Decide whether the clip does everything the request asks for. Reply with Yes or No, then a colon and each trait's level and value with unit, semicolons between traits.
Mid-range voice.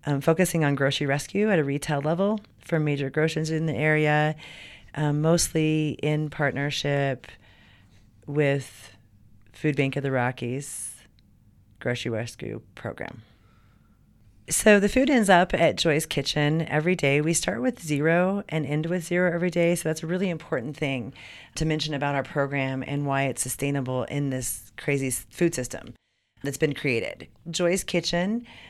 Yes: medium, 145 Hz